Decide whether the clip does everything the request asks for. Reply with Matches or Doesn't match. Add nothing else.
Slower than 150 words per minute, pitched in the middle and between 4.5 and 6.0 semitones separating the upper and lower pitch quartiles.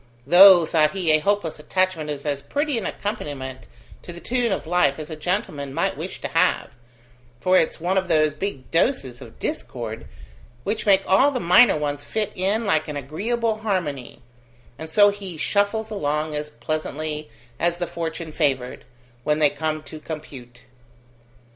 Doesn't match